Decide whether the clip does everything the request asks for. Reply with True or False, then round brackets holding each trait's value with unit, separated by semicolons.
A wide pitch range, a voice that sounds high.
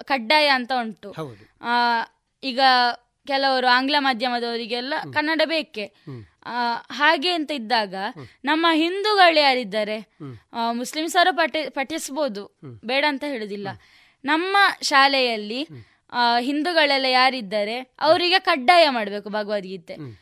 True (5.7 semitones; 260 Hz)